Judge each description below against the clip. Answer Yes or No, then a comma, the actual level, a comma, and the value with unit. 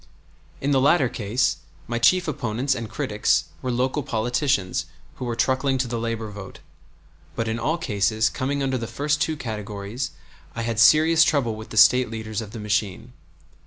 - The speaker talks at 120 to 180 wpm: Yes, average, 175 wpm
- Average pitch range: Yes, average, 3.4 semitones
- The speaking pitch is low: Yes, low, 120 Hz